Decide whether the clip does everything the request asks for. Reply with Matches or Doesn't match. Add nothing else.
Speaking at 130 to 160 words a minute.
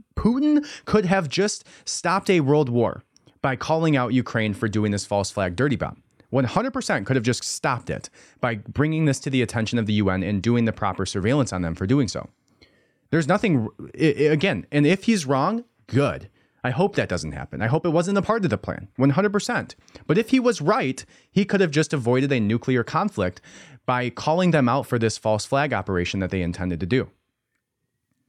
Doesn't match